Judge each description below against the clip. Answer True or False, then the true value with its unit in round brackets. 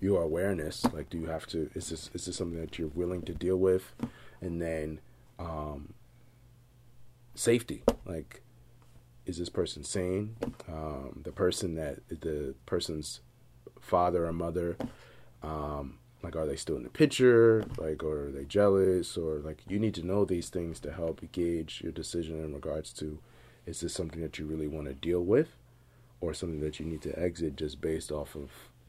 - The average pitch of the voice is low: True (85 Hz)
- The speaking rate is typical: True (180 wpm)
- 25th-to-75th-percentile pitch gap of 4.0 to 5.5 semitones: True (4.5 semitones)